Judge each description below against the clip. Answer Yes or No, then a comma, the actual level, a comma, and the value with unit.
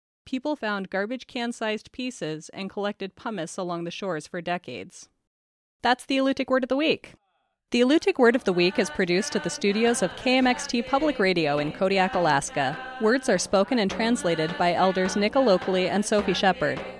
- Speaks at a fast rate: No, average, 175 wpm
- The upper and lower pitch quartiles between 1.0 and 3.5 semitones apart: No, average, 5.3 semitones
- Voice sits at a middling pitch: No, high, 200 Hz